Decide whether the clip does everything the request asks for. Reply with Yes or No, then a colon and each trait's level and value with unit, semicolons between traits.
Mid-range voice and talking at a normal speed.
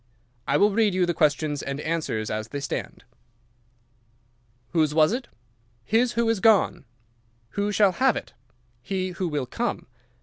Yes: medium, 180 Hz; average, 155 wpm